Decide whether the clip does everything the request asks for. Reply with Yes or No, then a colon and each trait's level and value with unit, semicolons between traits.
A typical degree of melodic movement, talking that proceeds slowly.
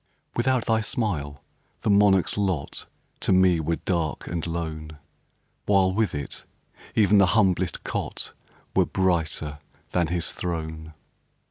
Yes: average, 3.8 semitones; slow, 125 wpm